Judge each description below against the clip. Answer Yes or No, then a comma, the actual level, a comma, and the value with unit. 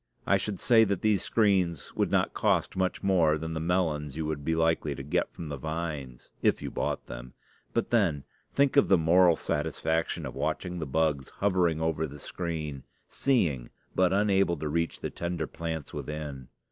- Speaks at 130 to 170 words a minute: No, average, 185 wpm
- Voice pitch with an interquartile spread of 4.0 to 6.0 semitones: No, average, 3.6 semitones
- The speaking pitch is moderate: No, very low, 80 Hz